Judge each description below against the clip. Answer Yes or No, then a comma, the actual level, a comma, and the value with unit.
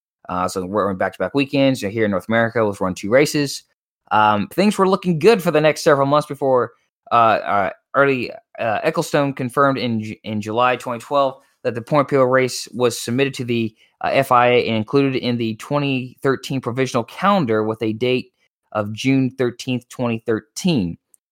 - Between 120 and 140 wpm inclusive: No, average, 175 wpm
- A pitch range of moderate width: Yes, average, 3.6 semitones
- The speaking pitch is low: Yes, low, 125 Hz